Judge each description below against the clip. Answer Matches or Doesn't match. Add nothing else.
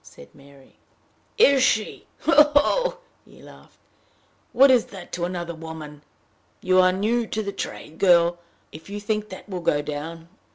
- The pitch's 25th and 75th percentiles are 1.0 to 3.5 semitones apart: Doesn't match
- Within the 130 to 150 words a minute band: Doesn't match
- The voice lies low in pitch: Doesn't match